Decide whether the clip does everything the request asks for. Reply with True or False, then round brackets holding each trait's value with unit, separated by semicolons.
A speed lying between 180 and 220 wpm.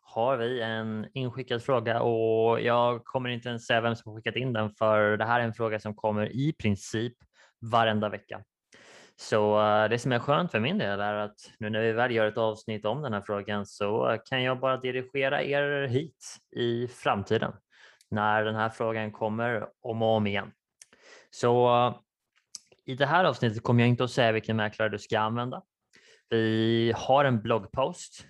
True (185 wpm)